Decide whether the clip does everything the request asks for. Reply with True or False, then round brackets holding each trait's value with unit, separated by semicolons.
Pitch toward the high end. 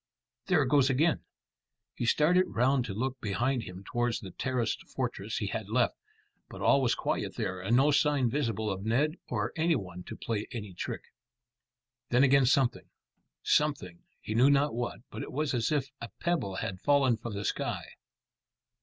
False (125 Hz)